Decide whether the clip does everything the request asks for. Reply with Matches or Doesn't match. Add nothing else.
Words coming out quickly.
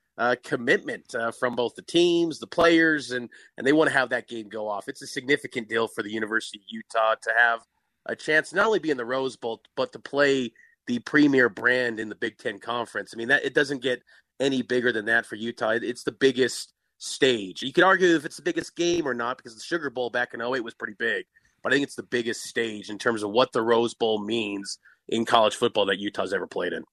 Matches